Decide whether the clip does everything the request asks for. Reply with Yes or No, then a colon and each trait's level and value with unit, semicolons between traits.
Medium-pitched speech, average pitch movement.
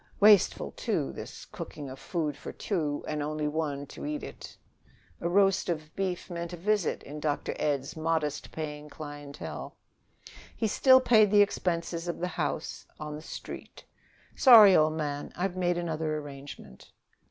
Yes: medium, 160 Hz; average, 3.7 semitones